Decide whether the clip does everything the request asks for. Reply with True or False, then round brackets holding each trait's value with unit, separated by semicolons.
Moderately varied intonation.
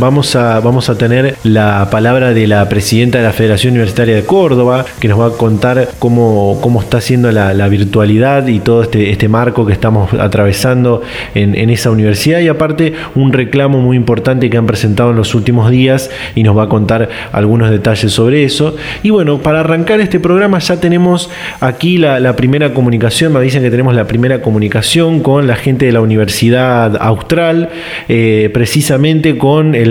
True (3.8 semitones)